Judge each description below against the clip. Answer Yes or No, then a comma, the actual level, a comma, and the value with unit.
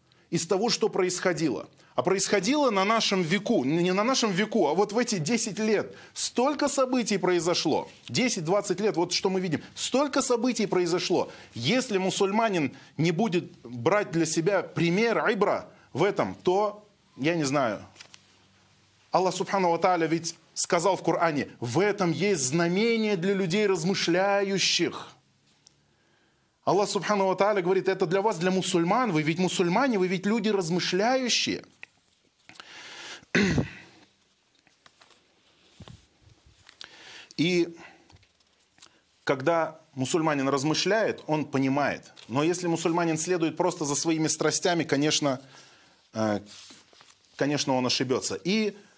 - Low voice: No, medium, 180 Hz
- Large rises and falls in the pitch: No, average, 4.2 semitones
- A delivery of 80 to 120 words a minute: Yes, average, 115 wpm